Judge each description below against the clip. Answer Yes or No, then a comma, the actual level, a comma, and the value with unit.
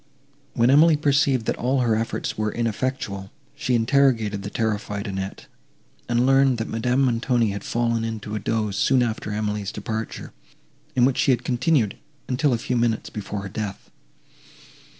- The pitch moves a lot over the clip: No, average, 3.3 semitones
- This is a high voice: No, low, 115 Hz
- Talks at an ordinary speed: Yes, average, 160 wpm